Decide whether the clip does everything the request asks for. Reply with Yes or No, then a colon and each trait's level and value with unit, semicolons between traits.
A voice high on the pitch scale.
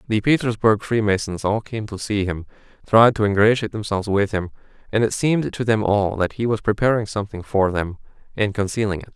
No: low, 105 Hz